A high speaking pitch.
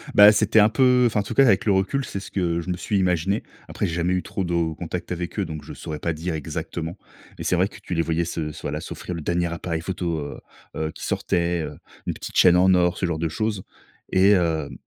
No: very low, 90 Hz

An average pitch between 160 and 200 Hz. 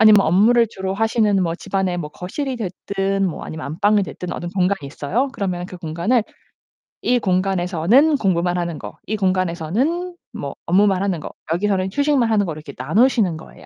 Yes: high, 190 Hz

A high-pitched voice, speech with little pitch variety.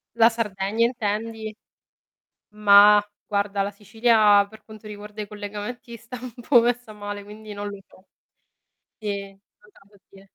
Yes: high, 210 Hz; narrow, 1.9 semitones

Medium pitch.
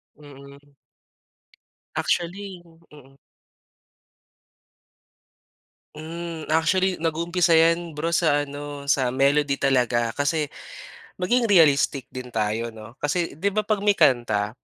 Yes: medium, 150 Hz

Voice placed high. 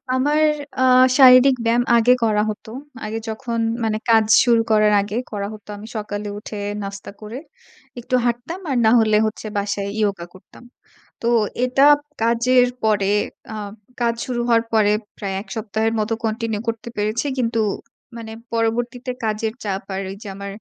Yes: high, 220 Hz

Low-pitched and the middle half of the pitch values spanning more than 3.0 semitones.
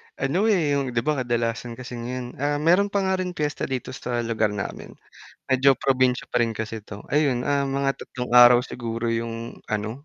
Yes: low, 125 Hz; average, 3.5 semitones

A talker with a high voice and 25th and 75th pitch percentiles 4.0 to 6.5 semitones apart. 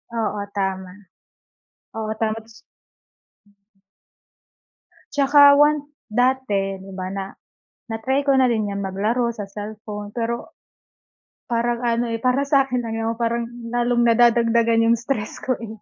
No: high, 230 Hz; narrow, 2.6 semitones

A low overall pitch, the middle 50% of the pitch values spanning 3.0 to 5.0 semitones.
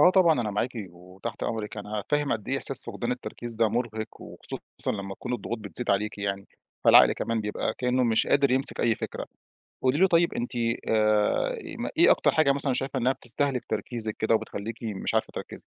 Yes: low, 115 Hz; average, 3.4 semitones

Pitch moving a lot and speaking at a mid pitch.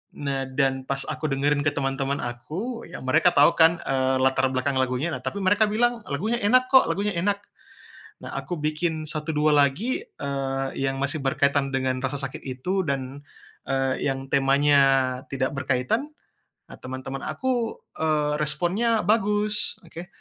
Yes: wide, 5.8 semitones; medium, 145 Hz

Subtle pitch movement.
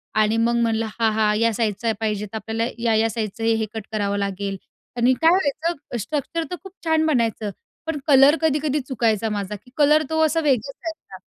No: wide, 5.4 semitones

